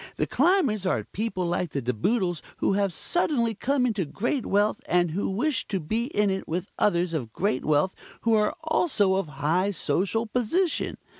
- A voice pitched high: Yes, high, 200 Hz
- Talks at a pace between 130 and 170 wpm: No, average, 180 wpm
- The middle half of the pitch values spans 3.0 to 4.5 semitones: No, average, 5.1 semitones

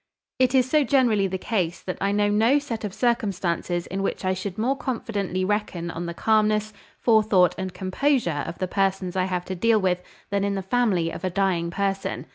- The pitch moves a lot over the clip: No, average, 3.2 semitones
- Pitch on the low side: No, high, 195 Hz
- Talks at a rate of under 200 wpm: No, fast, 205 wpm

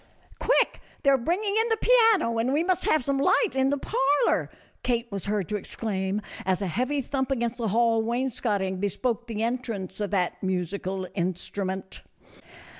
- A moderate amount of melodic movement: No, wide, 5.7 semitones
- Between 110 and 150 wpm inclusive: No, average, 175 wpm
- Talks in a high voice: Yes, high, 230 Hz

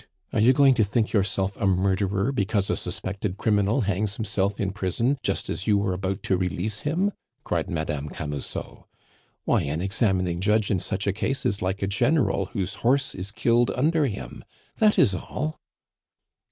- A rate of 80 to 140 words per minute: No, average, 175 wpm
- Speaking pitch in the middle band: No, low, 100 Hz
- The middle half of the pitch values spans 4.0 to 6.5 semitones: No, average, 3.5 semitones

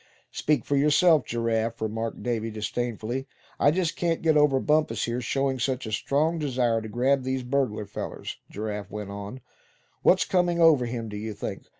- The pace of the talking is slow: No, average, 175 wpm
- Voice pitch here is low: Yes, low, 125 Hz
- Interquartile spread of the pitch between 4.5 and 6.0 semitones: Yes, average, 4.8 semitones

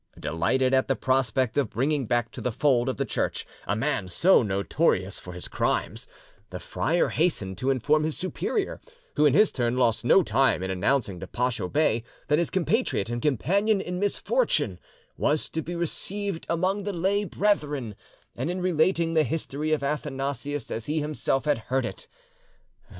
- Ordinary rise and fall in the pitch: No, wide, 5.9 semitones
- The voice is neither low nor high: Yes, medium, 145 Hz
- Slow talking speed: No, average, 175 wpm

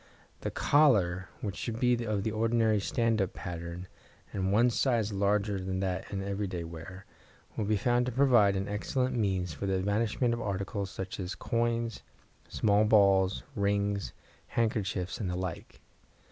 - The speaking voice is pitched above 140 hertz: No, low, 100 Hz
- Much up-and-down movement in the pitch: No, average, 3.2 semitones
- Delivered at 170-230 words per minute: No, average, 160 wpm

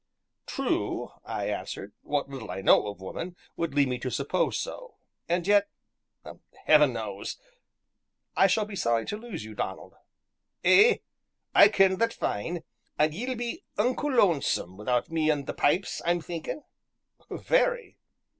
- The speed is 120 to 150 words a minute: Yes, average, 145 wpm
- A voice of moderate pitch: Yes, medium, 165 Hz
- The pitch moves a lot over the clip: Yes, wide, 8.4 semitones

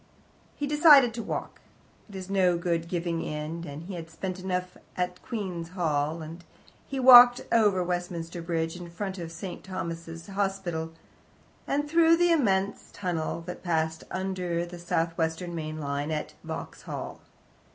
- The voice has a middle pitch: Yes, medium, 175 Hz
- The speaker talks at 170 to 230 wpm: No, average, 155 wpm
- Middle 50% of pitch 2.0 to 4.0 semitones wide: Yes, average, 2.8 semitones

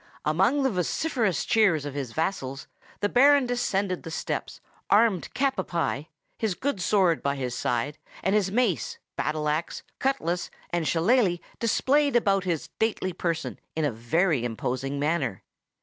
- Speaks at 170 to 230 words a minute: No, average, 150 wpm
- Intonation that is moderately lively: No, wide, 6.8 semitones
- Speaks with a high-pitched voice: No, medium, 175 Hz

